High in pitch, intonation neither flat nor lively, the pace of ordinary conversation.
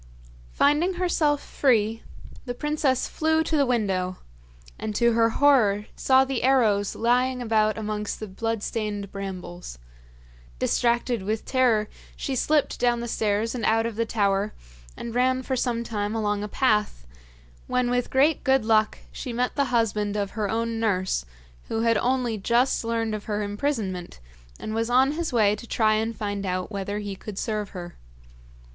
Yes: high, 225 Hz; average, 3.3 semitones; average, 165 wpm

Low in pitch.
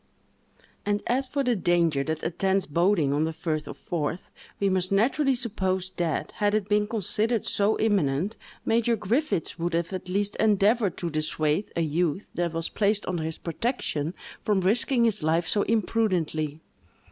No: high, 190 Hz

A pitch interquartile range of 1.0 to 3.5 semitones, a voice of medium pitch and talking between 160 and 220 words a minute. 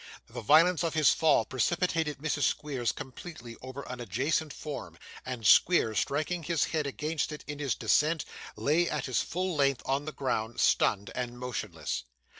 No: average, 4.2 semitones; medium, 145 Hz; average, 165 wpm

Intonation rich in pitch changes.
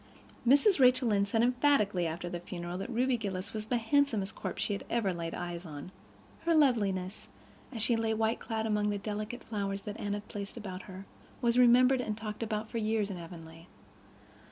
No: average, 3.8 semitones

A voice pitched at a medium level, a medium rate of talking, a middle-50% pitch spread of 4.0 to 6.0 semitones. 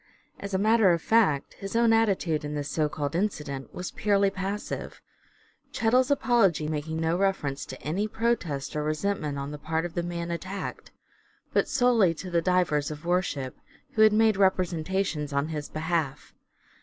Yes: medium, 175 Hz; average, 175 wpm; average, 4.8 semitones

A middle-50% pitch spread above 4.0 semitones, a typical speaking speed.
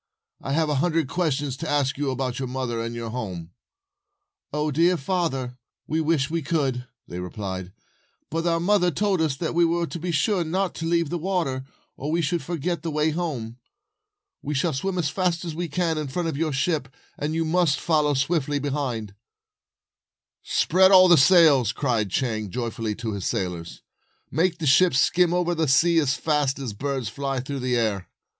Yes: average, 4.6 semitones; average, 190 wpm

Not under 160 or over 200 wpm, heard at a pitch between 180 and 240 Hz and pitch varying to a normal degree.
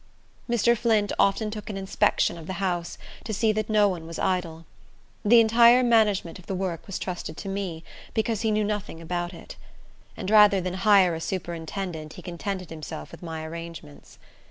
Yes: average, 180 wpm; high, 190 Hz; average, 4.0 semitones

